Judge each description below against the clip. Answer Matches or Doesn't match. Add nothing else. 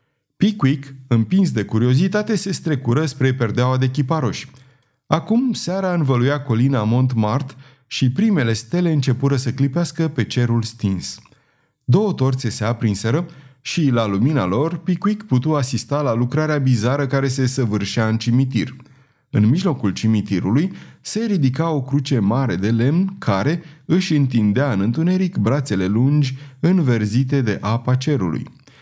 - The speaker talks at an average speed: Matches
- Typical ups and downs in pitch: Matches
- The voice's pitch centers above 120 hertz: Matches